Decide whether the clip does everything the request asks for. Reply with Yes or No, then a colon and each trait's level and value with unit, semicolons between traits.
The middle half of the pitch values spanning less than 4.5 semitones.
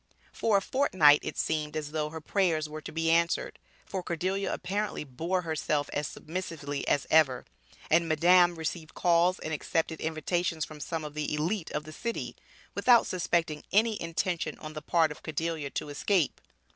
Yes: average, 2.7 semitones